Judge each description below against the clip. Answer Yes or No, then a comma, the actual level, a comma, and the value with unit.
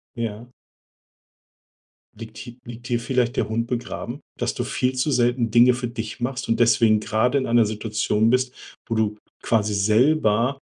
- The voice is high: No, low, 120 Hz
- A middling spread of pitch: No, narrow, 2.2 semitones